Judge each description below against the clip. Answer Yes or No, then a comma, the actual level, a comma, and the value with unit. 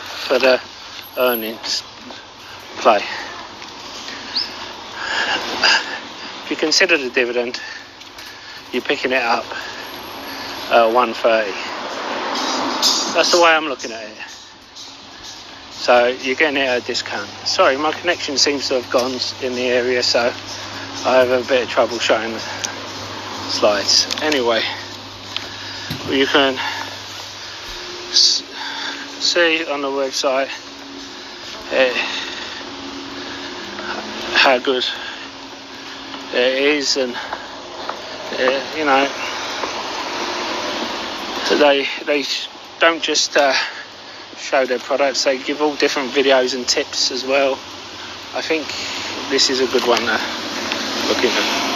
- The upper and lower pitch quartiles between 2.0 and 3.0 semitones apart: Yes, average, 2.7 semitones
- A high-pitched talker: No, low, 135 Hz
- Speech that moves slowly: Yes, slow, 105 wpm